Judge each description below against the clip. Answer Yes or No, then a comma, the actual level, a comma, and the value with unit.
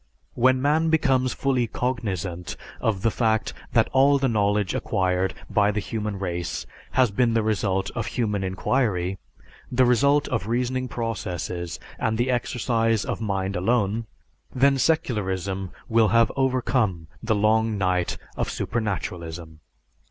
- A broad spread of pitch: No, average, 4.5 semitones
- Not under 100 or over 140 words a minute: Yes, slow, 135 wpm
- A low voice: Yes, low, 110 Hz